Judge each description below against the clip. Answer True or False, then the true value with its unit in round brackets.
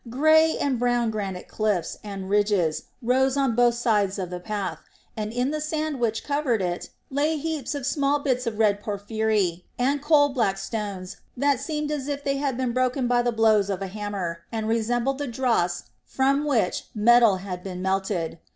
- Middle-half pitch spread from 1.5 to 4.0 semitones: False (5.3 semitones)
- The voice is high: True (230 Hz)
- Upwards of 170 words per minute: True (185 wpm)